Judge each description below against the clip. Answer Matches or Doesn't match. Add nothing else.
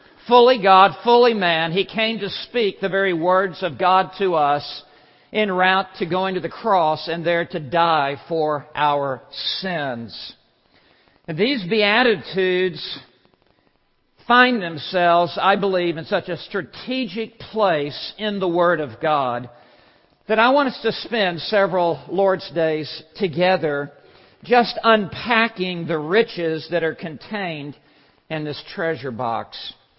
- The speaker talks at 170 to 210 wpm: Doesn't match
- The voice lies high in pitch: Doesn't match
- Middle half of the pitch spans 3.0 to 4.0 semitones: Doesn't match